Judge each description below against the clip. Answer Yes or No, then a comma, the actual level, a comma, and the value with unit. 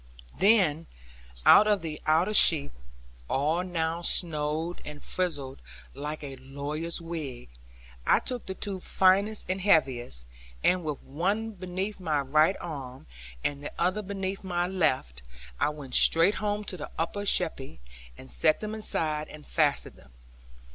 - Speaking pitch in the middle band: Yes, medium, 165 Hz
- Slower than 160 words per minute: Yes, average, 140 wpm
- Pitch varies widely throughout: No, average, 4.5 semitones